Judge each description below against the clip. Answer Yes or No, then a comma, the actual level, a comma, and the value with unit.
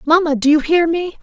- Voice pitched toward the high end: Yes, very high, 320 Hz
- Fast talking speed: Yes, fast, 245 wpm